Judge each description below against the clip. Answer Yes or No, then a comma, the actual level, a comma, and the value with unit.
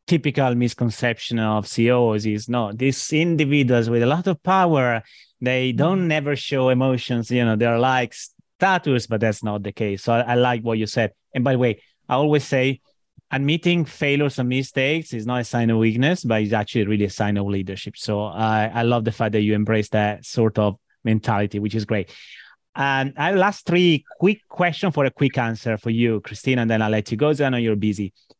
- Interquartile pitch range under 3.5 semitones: No, average, 4.0 semitones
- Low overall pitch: Yes, low, 120 Hz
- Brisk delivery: Yes, fast, 210 wpm